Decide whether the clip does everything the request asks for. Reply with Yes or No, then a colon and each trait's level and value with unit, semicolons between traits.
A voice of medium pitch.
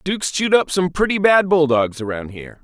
Yes: medium, 160 Hz